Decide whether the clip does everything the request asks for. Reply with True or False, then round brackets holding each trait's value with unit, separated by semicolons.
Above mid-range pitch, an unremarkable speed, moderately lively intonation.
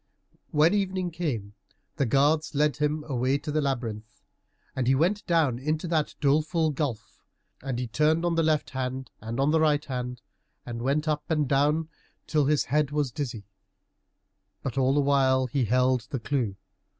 False (140 Hz; 175 wpm; 3.2 semitones)